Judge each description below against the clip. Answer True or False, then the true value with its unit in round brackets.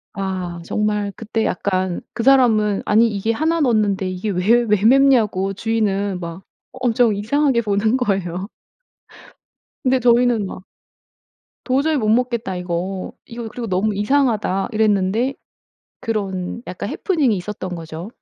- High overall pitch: True (215 Hz)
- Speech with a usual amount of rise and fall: True (3.8 semitones)